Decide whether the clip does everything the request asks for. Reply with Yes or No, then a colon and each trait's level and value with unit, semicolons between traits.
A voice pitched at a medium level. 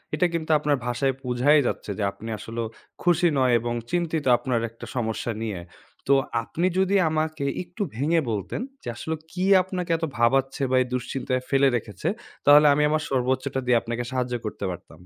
No: low, 130 Hz